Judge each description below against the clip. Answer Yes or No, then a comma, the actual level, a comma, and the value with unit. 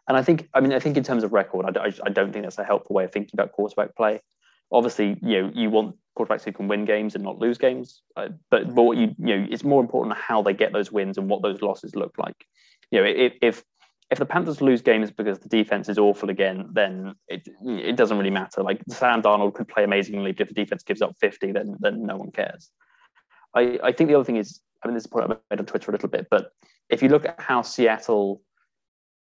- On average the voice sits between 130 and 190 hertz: No, low, 110 Hz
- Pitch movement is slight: No, average, 3.6 semitones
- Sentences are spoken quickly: Yes, fast, 255 wpm